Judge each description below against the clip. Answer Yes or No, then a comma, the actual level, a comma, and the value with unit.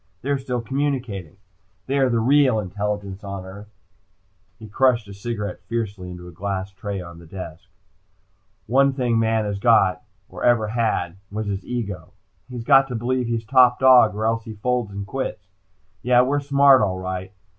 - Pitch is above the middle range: No, low, 110 Hz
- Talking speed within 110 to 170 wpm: No, average, 180 wpm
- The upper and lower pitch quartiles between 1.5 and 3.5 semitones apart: No, average, 4.2 semitones